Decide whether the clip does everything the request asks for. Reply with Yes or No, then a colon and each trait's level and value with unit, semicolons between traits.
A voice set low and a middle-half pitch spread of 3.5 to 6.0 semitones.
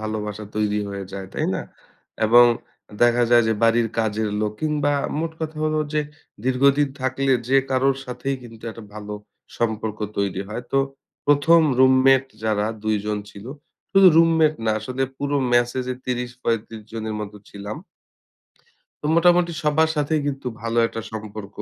Yes: low, 120 Hz; average, 4.6 semitones